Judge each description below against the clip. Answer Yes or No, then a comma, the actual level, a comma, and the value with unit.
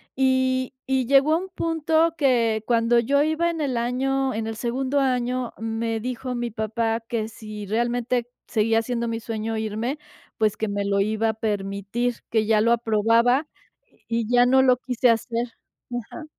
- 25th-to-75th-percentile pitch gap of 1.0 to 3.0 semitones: Yes, average, 2.7 semitones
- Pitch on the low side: No, high, 235 Hz